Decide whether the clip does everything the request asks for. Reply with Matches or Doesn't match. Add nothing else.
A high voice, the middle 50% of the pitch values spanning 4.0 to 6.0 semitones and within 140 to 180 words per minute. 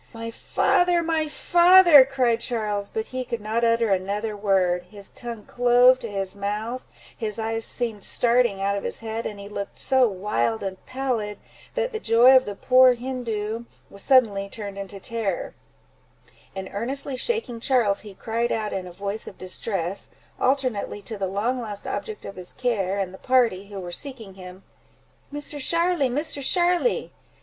Matches